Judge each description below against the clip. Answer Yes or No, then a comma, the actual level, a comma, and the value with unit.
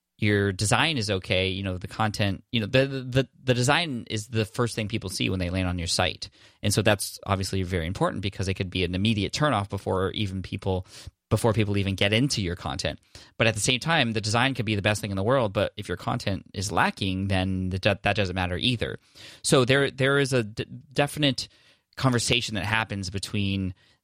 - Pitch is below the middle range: Yes, low, 105 Hz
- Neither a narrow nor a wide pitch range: Yes, average, 4.0 semitones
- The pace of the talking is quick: Yes, fast, 215 wpm